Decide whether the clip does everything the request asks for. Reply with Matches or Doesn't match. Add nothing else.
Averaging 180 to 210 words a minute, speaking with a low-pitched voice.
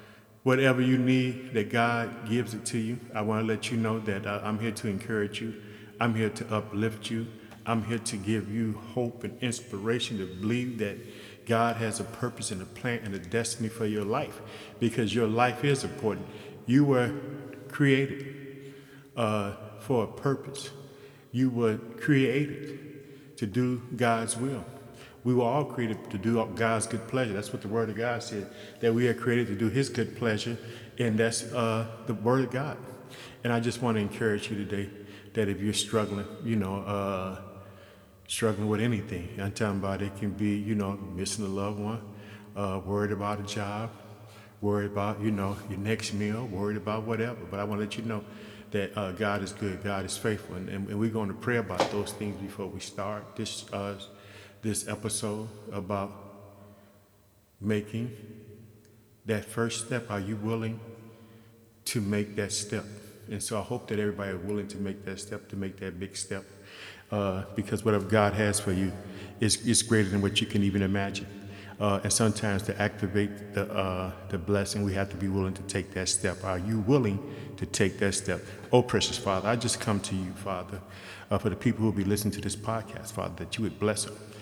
Matches